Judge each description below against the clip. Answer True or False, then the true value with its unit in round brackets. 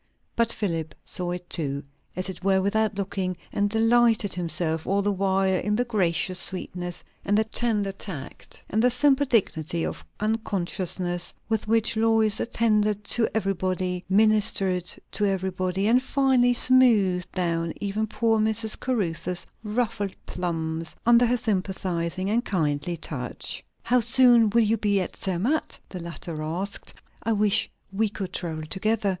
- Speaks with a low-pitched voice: False (200 Hz)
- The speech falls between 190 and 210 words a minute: False (145 wpm)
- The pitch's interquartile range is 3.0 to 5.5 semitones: True (3.7 semitones)